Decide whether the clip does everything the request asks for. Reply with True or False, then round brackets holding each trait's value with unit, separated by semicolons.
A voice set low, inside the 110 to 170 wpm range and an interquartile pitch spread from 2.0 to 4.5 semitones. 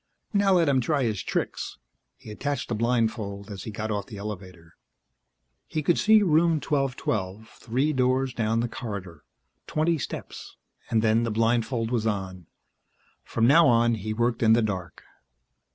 True (115 Hz; 160 wpm; 4.0 semitones)